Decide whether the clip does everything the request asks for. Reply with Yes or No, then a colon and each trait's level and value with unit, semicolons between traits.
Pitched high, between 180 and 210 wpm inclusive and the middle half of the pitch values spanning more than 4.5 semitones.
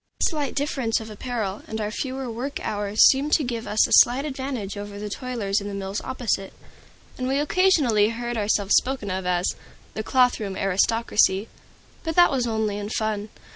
No: high, 225 Hz; average, 185 wpm; average, 4.2 semitones